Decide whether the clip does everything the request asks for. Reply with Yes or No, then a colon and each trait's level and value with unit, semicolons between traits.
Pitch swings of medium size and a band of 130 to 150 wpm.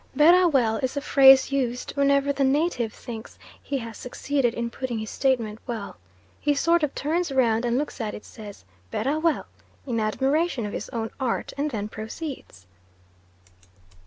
No: average, 3.9 semitones; average, 165 wpm